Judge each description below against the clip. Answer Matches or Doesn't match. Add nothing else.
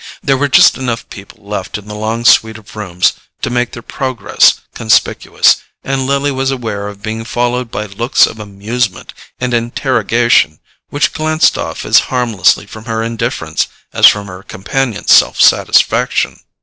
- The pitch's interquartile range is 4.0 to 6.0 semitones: Doesn't match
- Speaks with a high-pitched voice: Doesn't match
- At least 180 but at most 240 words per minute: Doesn't match